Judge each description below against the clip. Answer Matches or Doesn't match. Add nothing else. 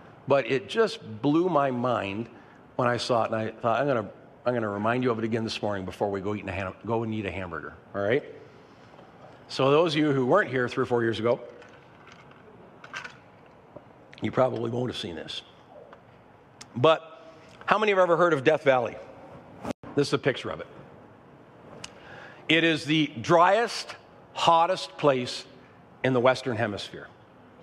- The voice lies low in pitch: Matches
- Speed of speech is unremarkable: Matches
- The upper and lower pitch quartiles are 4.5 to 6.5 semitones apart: Matches